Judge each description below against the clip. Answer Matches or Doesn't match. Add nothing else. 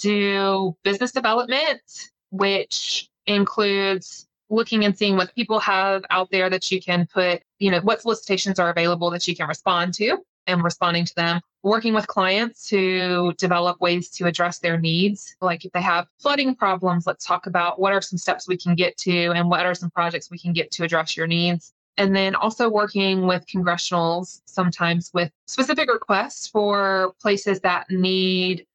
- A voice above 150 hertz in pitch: Matches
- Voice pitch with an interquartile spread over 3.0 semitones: Doesn't match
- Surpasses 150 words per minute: Matches